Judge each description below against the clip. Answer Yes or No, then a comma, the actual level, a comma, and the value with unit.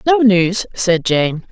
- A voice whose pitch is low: No, high, 195 Hz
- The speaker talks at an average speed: Yes, average, 160 wpm